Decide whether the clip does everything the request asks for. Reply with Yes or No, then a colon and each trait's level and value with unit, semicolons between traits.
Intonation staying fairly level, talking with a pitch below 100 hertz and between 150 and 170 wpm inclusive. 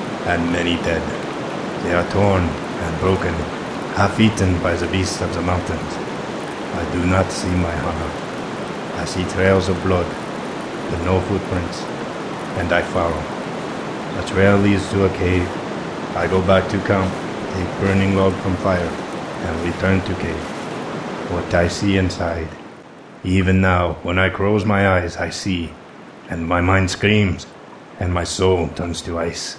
Yes: narrow, 2.0 semitones; very low, 90 Hz; average, 155 wpm